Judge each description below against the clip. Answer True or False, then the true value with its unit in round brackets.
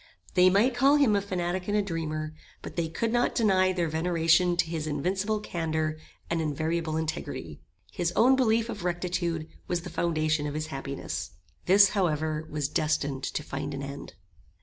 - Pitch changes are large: False (3.4 semitones)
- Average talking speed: True (170 wpm)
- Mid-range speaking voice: True (165 Hz)